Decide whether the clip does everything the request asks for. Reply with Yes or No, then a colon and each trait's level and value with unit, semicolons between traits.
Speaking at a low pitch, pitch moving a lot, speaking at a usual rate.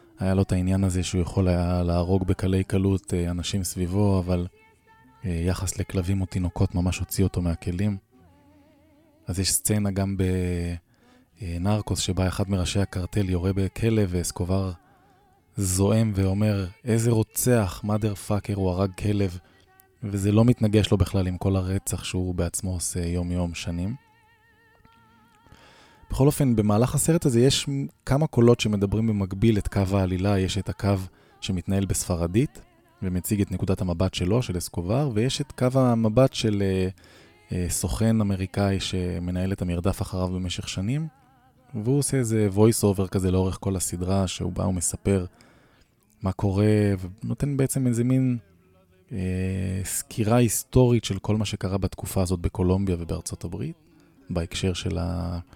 No: very low, 95 Hz; average, 3.1 semitones; average, 140 wpm